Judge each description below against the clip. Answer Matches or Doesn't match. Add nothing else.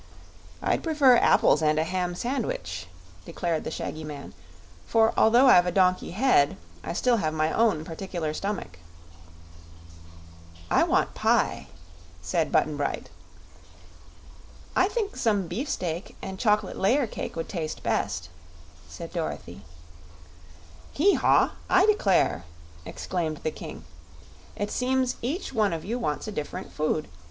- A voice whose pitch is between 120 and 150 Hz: Doesn't match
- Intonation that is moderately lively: Doesn't match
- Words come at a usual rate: Doesn't match